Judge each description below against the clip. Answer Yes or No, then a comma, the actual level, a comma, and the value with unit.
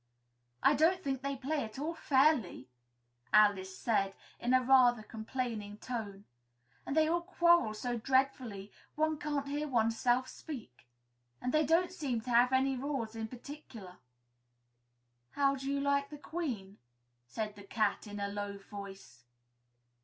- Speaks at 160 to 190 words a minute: No, average, 145 wpm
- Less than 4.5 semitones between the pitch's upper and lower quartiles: No, average, 5.1 semitones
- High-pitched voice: Yes, very high, 250 Hz